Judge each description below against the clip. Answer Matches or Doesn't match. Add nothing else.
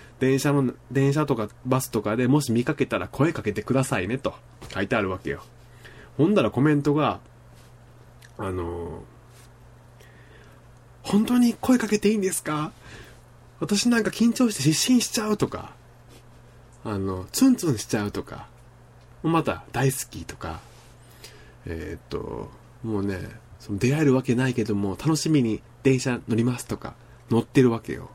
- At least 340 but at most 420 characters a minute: Doesn't match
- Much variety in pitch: Doesn't match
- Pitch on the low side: Matches